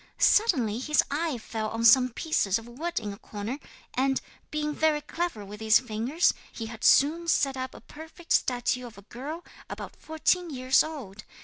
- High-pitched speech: Yes, very high, 260 Hz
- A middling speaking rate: Yes, average, 180 wpm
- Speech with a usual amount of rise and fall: No, wide, 5.7 semitones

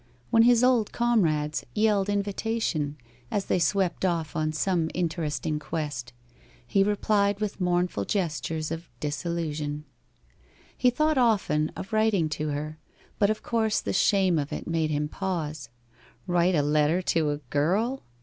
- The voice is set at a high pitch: No, medium, 170 Hz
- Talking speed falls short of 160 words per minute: Yes, average, 145 wpm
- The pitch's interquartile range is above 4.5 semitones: Yes, average, 5.2 semitones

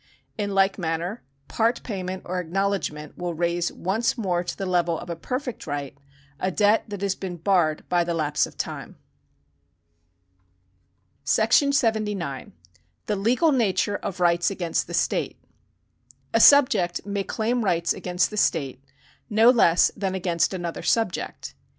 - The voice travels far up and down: No, average, 3.6 semitones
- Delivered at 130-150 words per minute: Yes, average, 145 wpm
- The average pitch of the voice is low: No, high, 190 Hz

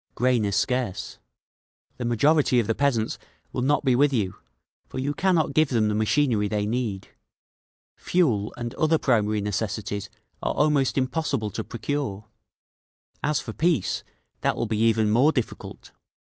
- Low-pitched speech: Yes, low, 120 Hz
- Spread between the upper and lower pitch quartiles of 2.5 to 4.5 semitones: No, average, 5.0 semitones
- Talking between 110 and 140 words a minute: No, average, 150 wpm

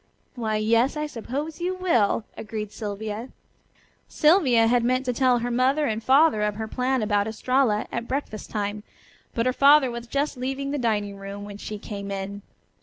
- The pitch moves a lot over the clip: No, average, 4.0 semitones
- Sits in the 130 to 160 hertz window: No, high, 235 Hz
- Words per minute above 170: Yes, average, 180 wpm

